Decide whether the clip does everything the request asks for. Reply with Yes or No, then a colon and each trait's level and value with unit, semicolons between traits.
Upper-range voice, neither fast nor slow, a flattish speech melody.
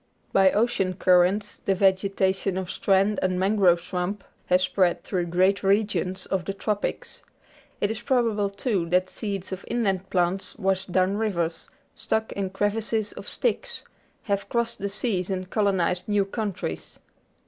Yes: high, 195 Hz; average, 150 wpm; narrow, 2.0 semitones